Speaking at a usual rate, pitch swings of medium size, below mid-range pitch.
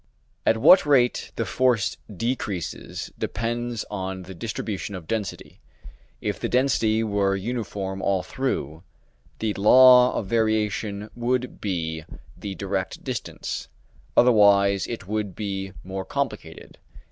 No: slow, 120 wpm; average, 3.4 semitones; low, 105 Hz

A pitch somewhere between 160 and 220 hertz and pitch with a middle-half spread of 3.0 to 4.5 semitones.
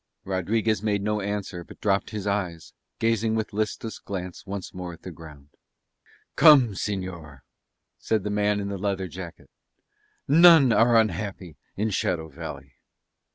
No: low, 100 Hz; average, 3.3 semitones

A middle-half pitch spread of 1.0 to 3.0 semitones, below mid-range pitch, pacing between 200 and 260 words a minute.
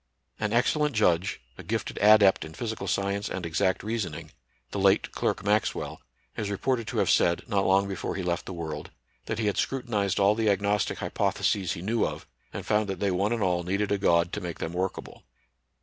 Yes: average, 2.7 semitones; low, 100 Hz; fast, 205 wpm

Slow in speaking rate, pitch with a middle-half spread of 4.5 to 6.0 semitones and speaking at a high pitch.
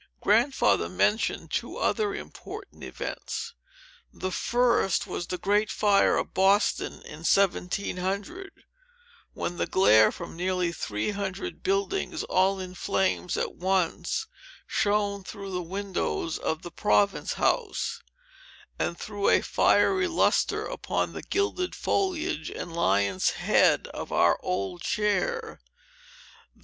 Yes: slow, 120 wpm; average, 5.2 semitones; high, 195 Hz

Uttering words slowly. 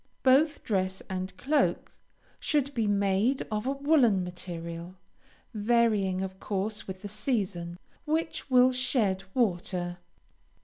Yes: slow, 120 wpm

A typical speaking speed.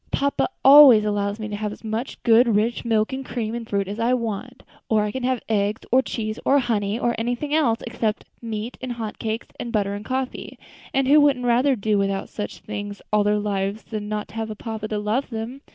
No: fast, 220 wpm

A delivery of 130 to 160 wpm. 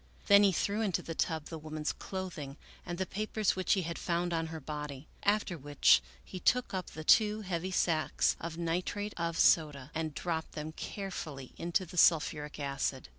No: average, 180 wpm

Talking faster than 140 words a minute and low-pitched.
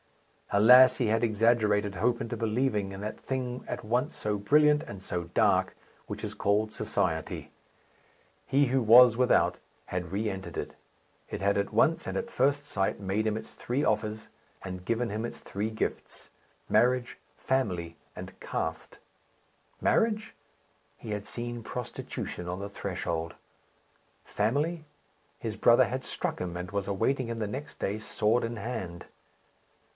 Yes: average, 150 wpm; low, 110 Hz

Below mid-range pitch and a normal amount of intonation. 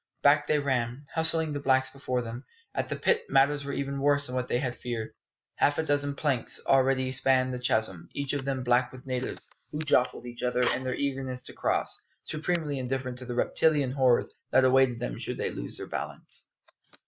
No: low, 130 Hz; narrow, 2.2 semitones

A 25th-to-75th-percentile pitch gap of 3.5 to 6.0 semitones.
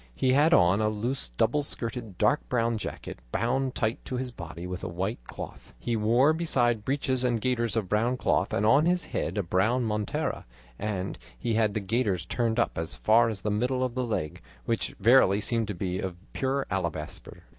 Yes: average, 4.4 semitones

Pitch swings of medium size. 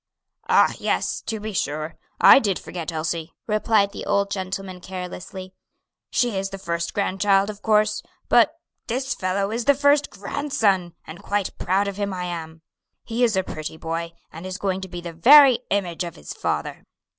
Yes: average, 3.5 semitones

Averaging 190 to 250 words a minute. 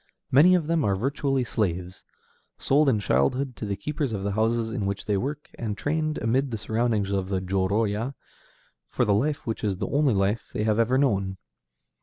Yes: average, 195 wpm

